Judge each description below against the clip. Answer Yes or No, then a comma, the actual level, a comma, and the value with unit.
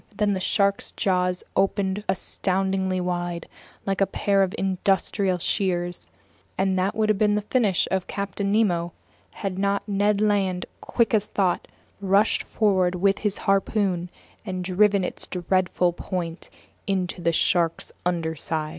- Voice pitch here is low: No, high, 190 Hz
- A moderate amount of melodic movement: No, narrow, 1.9 semitones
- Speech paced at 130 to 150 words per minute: Yes, average, 140 wpm